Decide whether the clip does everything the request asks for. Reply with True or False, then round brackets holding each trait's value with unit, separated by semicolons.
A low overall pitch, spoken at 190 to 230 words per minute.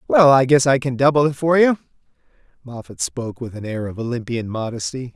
True (130 Hz; 200 wpm)